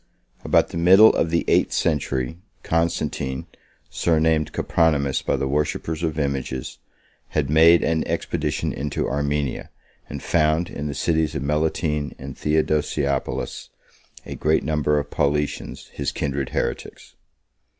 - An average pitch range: No, narrow, 2.2 semitones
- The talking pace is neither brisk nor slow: No, slow, 130 wpm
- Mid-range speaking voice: No, very low, 75 Hz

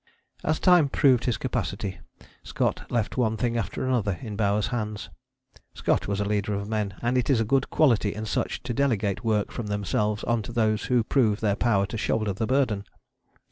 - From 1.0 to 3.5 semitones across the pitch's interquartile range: Yes, average, 3.0 semitones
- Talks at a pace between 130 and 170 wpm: No, average, 195 wpm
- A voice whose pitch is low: Yes, low, 110 Hz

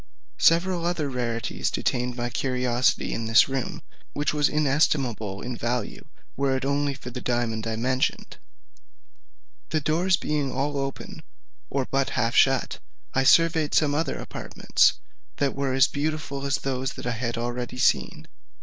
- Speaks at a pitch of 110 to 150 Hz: Yes, low, 135 Hz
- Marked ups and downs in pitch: No, average, 2.9 semitones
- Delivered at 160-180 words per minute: No, average, 150 wpm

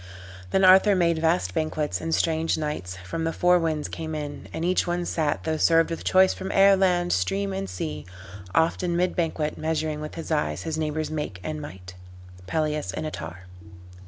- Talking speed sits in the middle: Yes, average, 190 wpm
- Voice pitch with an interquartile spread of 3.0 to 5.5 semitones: No, narrow, 2.5 semitones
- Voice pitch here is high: No, medium, 160 Hz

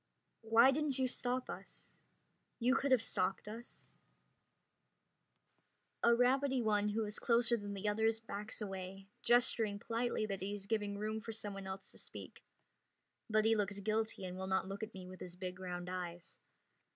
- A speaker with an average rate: Yes, average, 170 wpm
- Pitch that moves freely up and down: No, average, 3.1 semitones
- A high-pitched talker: Yes, high, 215 Hz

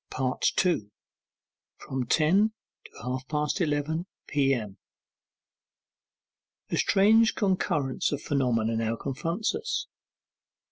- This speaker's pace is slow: Yes, slow, 90 wpm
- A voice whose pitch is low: No, medium, 145 Hz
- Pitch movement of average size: No, wide, 6.5 semitones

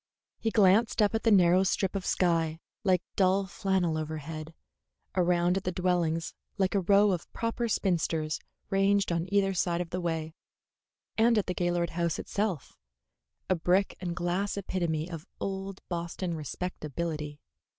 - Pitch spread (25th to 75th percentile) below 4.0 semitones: Yes, average, 2.7 semitones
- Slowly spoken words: No, average, 150 wpm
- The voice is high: No, medium, 180 Hz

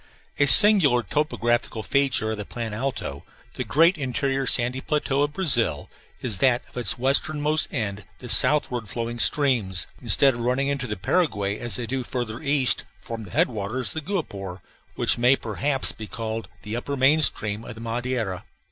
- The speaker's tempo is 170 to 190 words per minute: Yes, average, 175 wpm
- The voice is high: No, low, 125 Hz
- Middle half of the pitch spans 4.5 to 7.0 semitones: No, average, 3.9 semitones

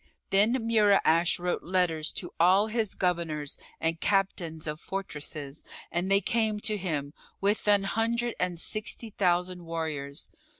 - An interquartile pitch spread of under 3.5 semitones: No, average, 4.2 semitones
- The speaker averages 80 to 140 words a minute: Yes, slow, 135 wpm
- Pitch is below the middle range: No, medium, 180 Hz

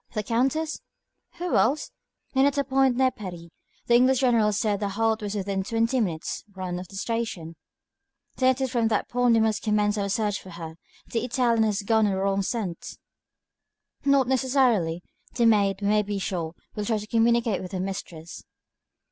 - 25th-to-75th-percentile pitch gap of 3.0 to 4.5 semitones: Yes, average, 3.9 semitones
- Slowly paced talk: No, average, 190 wpm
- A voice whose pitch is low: No, high, 215 Hz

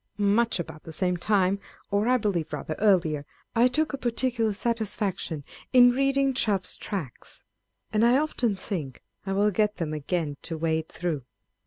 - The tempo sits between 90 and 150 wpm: No, average, 160 wpm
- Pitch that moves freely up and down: Yes, wide, 5.8 semitones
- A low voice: No, high, 200 Hz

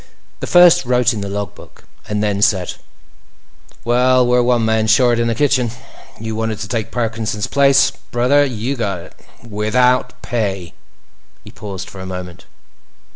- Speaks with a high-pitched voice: No, low, 115 Hz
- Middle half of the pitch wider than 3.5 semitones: No, average, 3.2 semitones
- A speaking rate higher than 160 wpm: No, average, 155 wpm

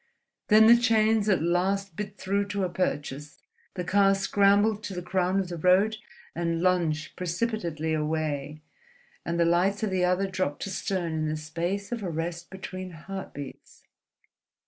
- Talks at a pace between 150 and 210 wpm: Yes, average, 160 wpm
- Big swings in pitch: No, average, 3.2 semitones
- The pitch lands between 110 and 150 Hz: No, medium, 185 Hz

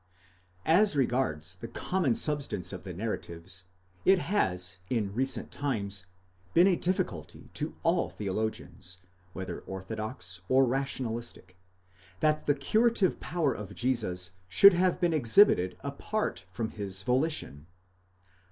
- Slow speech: Yes, slow, 120 wpm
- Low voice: Yes, low, 115 Hz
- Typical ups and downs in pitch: No, wide, 8.4 semitones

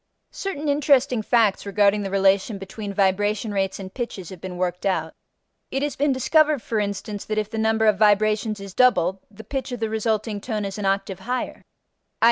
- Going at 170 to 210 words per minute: Yes, average, 195 wpm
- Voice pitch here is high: Yes, high, 210 Hz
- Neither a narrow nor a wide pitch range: Yes, average, 3.1 semitones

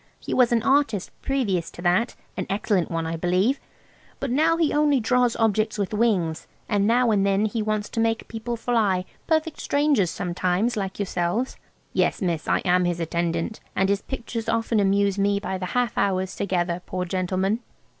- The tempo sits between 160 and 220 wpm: Yes, average, 170 wpm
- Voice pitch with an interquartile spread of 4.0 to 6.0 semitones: Yes, average, 4.4 semitones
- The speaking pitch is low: No, high, 205 Hz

